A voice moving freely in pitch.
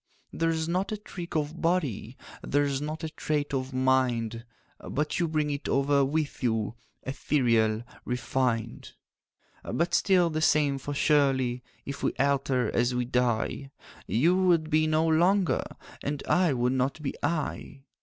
No: average, 3.9 semitones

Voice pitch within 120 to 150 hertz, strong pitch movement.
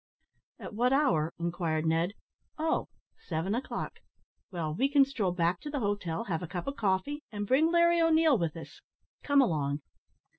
No: high, 200 Hz; wide, 8.9 semitones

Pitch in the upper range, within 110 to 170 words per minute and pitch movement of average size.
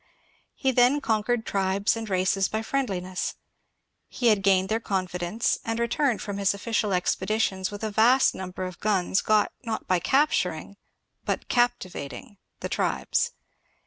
Yes: high, 205 Hz; average, 145 wpm; average, 3.5 semitones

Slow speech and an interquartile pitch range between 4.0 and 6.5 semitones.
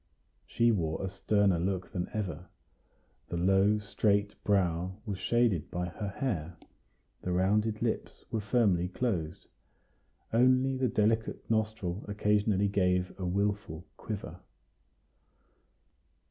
No: slow, 115 wpm; average, 3.0 semitones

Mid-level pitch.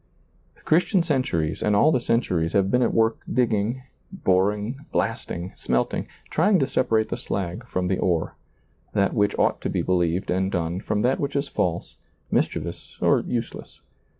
No: low, 105 Hz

